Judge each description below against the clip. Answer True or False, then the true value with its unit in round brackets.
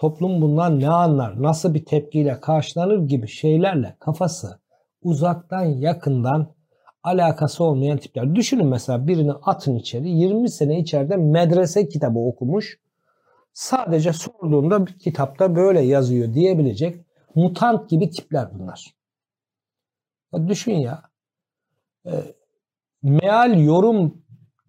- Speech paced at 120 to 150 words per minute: False (100 wpm)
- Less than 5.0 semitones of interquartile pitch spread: True (4.2 semitones)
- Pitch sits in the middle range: True (160 Hz)